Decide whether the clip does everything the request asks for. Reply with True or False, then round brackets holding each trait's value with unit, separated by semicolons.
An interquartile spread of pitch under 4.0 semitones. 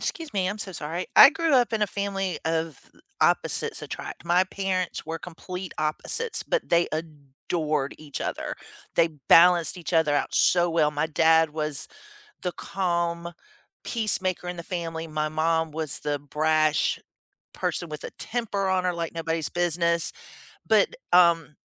True (2.8 semitones)